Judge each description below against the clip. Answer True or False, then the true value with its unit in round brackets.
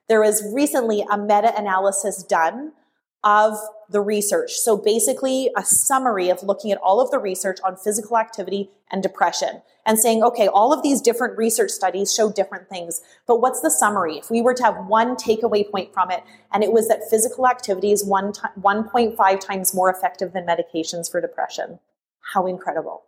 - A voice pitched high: True (210 Hz)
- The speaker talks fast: False (180 wpm)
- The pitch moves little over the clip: False (3.3 semitones)